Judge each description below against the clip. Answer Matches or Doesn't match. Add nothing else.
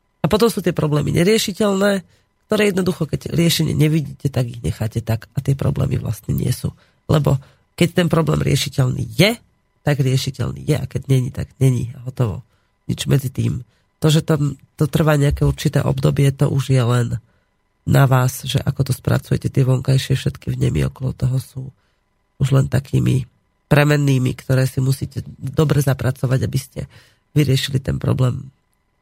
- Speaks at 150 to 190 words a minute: Matches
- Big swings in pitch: Doesn't match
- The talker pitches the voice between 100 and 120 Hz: Doesn't match